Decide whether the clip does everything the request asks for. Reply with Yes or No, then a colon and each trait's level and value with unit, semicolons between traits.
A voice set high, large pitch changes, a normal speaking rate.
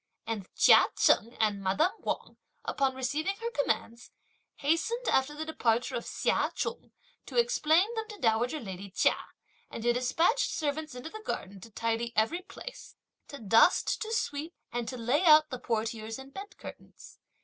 Yes: very high, 265 Hz; wide, 6.2 semitones; average, 165 wpm